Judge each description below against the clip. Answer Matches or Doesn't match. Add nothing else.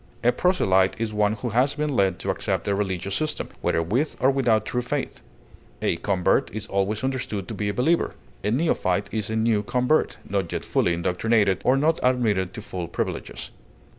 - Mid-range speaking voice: Doesn't match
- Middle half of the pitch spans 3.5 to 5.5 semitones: Matches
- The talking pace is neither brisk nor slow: Matches